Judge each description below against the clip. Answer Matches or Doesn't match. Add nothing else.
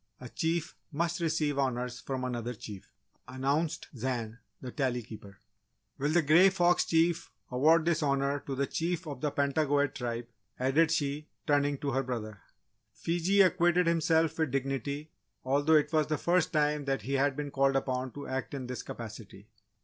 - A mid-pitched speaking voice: Matches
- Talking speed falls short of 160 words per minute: Doesn't match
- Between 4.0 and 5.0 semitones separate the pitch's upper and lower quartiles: Doesn't match